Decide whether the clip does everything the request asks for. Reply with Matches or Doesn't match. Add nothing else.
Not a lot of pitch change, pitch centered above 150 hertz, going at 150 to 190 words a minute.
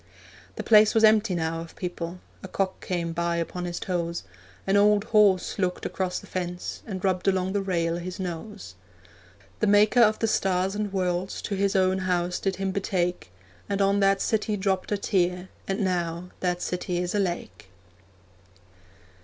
Matches